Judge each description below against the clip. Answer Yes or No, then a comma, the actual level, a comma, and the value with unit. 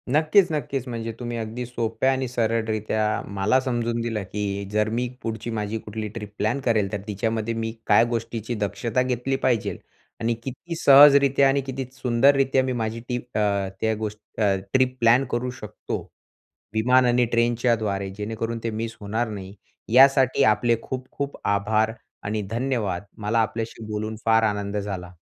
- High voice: No, low, 115 Hz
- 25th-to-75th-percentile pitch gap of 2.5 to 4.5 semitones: Yes, average, 2.9 semitones